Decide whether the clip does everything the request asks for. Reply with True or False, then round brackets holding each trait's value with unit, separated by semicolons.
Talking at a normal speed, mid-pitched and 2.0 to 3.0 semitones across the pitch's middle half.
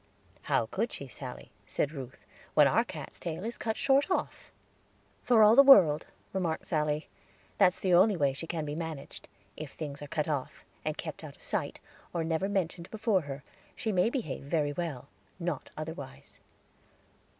False (170 wpm; 165 Hz; 4.8 semitones)